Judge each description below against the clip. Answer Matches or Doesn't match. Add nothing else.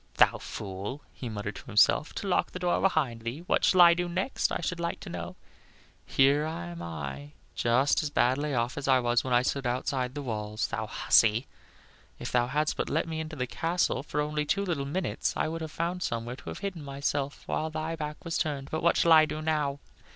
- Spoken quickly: Matches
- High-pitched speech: Doesn't match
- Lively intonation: Doesn't match